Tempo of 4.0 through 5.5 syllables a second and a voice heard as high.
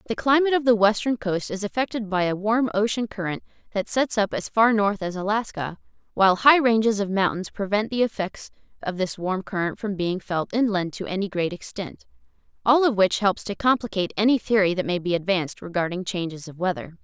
No: 5.7 syllables/s; high, 205 Hz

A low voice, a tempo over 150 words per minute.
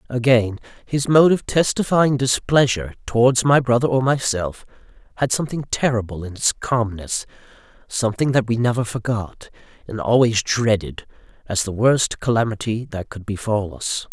No: low, 115 Hz; average, 140 wpm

